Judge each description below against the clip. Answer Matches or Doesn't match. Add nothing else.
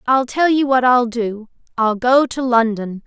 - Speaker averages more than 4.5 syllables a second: Doesn't match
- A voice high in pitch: Matches